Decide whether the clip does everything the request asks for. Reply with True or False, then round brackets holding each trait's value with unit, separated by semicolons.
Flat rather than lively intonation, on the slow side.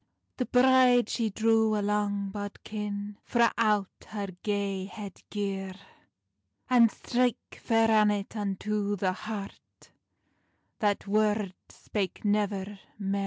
True (1.6 semitones; 115 wpm)